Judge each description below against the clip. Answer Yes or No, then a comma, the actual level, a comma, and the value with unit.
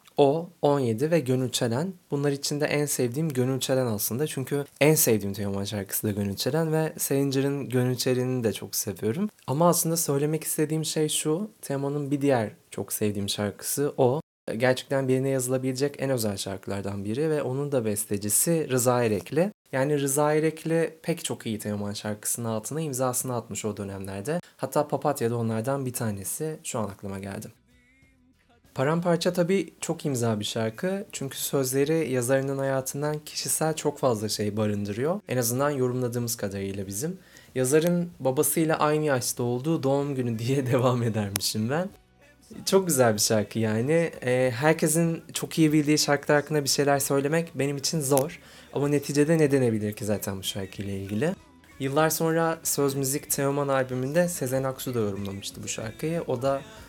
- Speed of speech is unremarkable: No, fast, 155 wpm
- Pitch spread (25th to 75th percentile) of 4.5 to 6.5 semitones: Yes, average, 5.2 semitones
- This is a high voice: No, low, 135 Hz